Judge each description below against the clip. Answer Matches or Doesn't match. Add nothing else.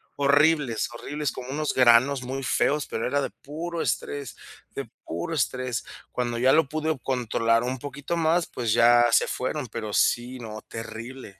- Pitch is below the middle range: Matches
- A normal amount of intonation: Matches